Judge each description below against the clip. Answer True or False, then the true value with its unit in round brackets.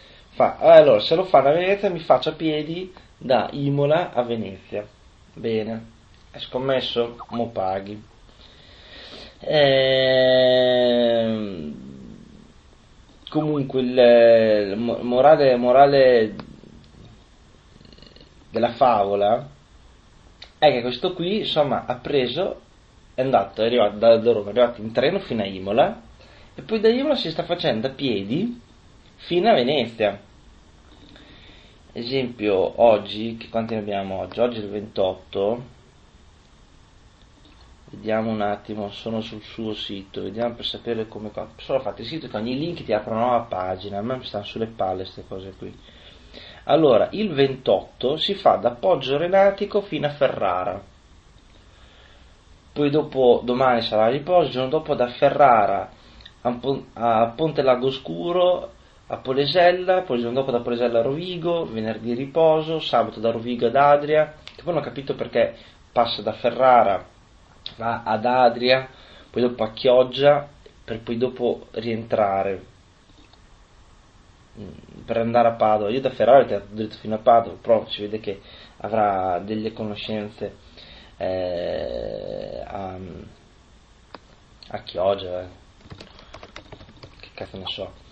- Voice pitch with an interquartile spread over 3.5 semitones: True (4.6 semitones)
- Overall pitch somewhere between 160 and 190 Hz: False (115 Hz)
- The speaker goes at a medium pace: True (130 wpm)